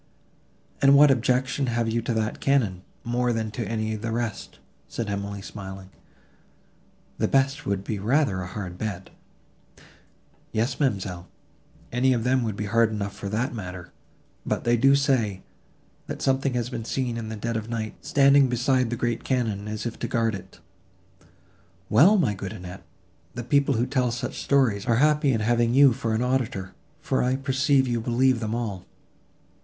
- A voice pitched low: Yes, low, 115 Hz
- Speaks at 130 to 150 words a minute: No, average, 175 wpm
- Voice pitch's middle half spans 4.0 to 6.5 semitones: No, average, 3.6 semitones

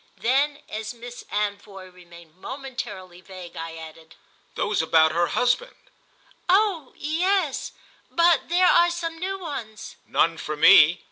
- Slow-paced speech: Yes, slow, 130 wpm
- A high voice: Yes, high, 225 Hz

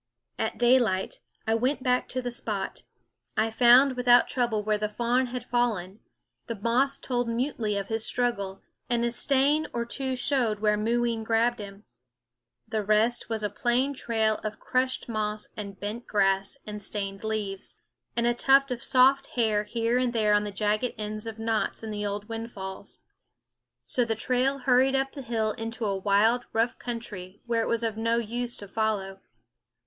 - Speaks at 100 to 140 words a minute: No, average, 175 wpm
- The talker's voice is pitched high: Yes, high, 225 Hz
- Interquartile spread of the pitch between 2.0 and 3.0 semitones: Yes, narrow, 2.6 semitones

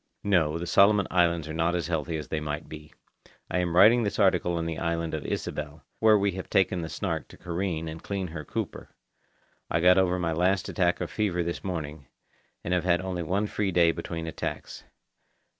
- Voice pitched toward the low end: Yes, very low, 85 Hz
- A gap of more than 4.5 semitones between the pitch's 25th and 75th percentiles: No, narrow, 2.5 semitones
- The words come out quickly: Yes, fast, 210 wpm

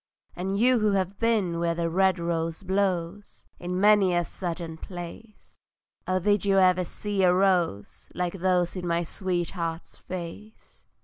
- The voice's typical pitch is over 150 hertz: Yes, medium, 185 Hz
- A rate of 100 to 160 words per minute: Yes, average, 150 wpm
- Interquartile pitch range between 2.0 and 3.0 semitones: Yes, narrow, 2.5 semitones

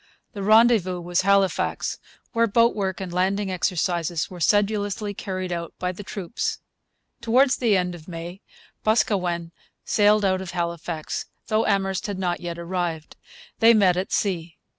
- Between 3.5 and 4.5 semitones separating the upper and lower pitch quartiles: No, average, 2.8 semitones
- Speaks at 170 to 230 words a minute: No, average, 150 wpm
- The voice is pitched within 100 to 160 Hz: No, medium, 185 Hz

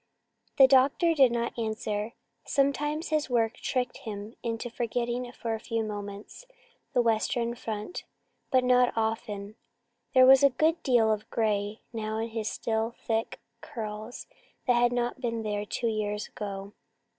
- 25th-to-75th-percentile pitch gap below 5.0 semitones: Yes, narrow, 2.5 semitones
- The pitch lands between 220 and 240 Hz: Yes, high, 230 Hz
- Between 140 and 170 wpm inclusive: Yes, average, 150 wpm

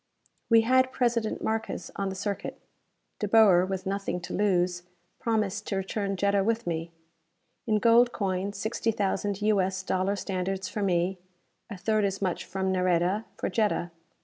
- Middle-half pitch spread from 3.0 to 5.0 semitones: No, narrow, 2.5 semitones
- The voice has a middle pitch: No, high, 195 Hz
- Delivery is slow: No, average, 160 wpm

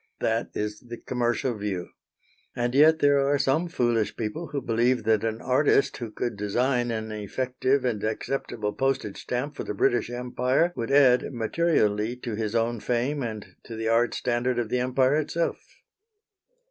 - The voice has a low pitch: Yes, low, 120 Hz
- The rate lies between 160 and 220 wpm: Yes, average, 165 wpm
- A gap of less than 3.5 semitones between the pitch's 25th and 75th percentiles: Yes, average, 3.1 semitones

